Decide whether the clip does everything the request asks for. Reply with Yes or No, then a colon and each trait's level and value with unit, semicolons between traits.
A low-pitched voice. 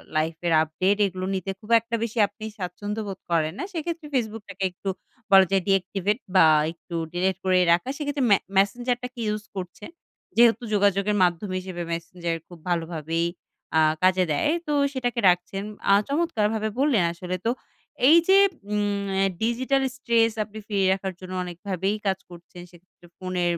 No: high, 195 Hz